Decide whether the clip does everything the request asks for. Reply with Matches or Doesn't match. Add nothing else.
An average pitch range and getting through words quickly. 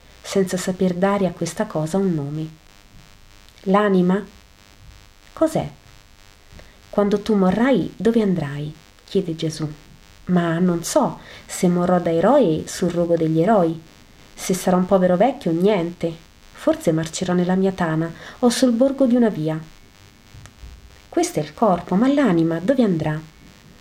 Doesn't match